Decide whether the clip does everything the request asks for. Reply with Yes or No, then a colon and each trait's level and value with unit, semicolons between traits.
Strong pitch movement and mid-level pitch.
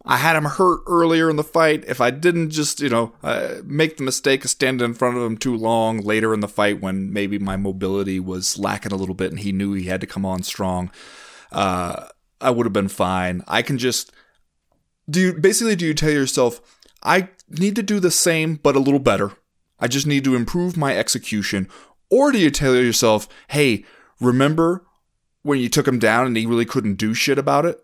No: wide, 6.8 semitones; low, 125 Hz